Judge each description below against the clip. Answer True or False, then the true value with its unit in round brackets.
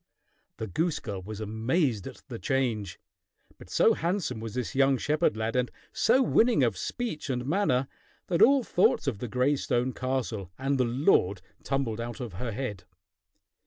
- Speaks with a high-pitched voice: False (125 Hz)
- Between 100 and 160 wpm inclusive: False (170 wpm)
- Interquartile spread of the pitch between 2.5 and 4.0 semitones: False (4.7 semitones)